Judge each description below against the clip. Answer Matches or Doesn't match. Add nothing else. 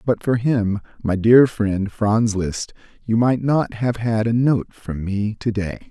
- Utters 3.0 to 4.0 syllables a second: Matches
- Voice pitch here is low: Matches